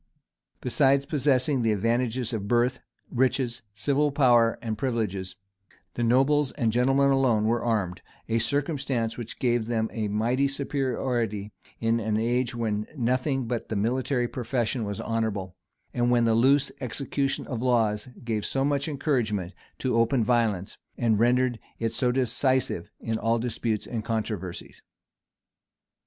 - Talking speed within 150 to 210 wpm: No, average, 140 wpm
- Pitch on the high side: No, low, 120 Hz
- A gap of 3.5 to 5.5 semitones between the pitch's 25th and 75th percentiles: No, average, 2.8 semitones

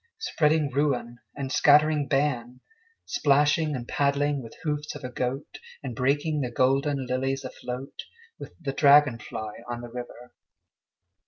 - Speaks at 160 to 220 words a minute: No, average, 140 wpm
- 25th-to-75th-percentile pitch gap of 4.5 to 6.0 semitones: No, average, 2.8 semitones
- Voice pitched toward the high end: No, low, 135 Hz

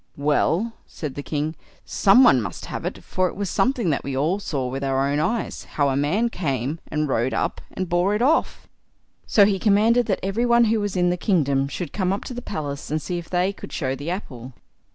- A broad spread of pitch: Yes, wide, 6.3 semitones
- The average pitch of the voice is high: No, medium, 175 Hz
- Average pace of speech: No, fast, 230 wpm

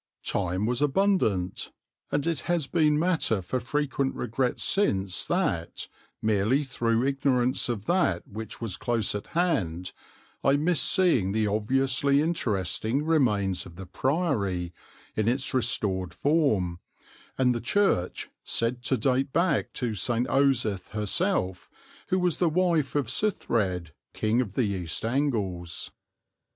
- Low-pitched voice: Yes, low, 120 Hz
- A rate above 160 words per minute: No, slow, 135 wpm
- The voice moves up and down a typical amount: No, wide, 6.7 semitones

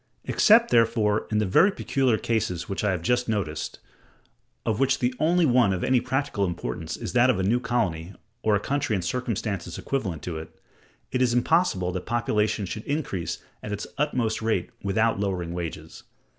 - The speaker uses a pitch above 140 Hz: No, low, 110 Hz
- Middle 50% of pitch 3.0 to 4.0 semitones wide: No, average, 5.1 semitones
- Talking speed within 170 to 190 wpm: Yes, average, 180 wpm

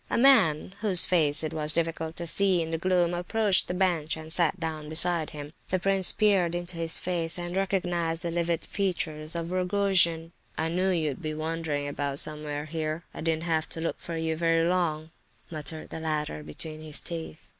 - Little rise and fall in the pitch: Yes, narrow, 2.2 semitones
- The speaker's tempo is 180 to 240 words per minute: Yes, average, 190 wpm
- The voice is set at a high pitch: No, medium, 165 Hz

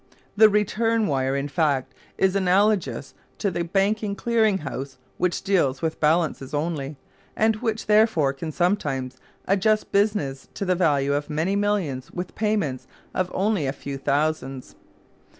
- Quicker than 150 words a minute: No, average, 145 wpm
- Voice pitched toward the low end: No, medium, 175 Hz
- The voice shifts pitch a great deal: Yes, wide, 6.7 semitones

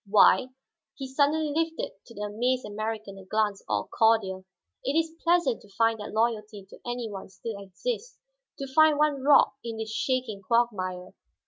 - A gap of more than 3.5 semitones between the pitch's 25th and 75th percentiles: Yes, average, 5.0 semitones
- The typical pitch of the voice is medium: No, high, 225 Hz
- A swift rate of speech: No, average, 165 wpm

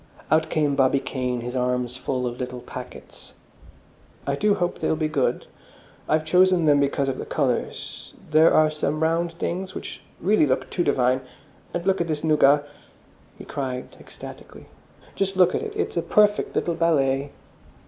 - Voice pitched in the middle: Yes, medium, 150 Hz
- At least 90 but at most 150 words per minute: No, average, 170 wpm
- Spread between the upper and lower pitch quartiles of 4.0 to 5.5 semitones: Yes, average, 4.5 semitones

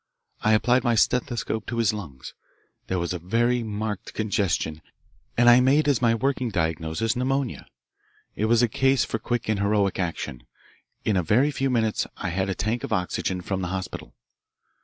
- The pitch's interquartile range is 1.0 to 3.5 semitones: No, average, 4.3 semitones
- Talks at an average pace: Yes, average, 180 wpm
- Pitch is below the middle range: Yes, low, 110 Hz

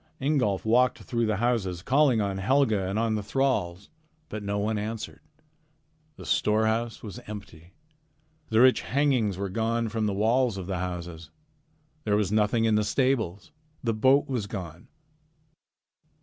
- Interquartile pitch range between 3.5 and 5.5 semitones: No, average, 3.1 semitones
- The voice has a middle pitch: No, low, 110 Hz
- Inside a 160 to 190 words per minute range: No, average, 150 wpm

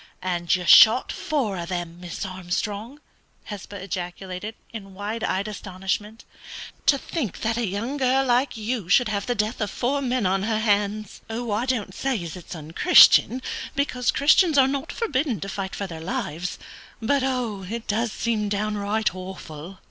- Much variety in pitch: No, average, 4.6 semitones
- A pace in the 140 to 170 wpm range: Yes, average, 165 wpm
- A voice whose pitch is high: Yes, high, 210 Hz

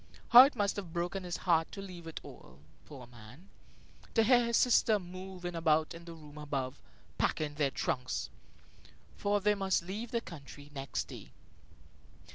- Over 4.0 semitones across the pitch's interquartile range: Yes, average, 5.1 semitones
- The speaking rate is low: No, average, 165 wpm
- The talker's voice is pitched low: No, medium, 175 Hz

